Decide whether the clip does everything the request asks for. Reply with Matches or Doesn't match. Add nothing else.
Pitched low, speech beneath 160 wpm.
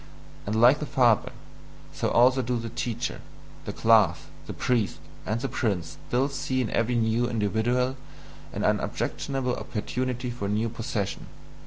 Matches